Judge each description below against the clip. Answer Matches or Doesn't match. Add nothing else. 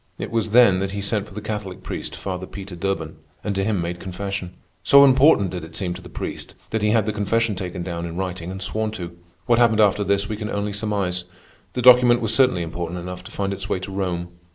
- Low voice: Matches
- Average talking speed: Doesn't match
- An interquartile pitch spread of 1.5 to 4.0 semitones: Matches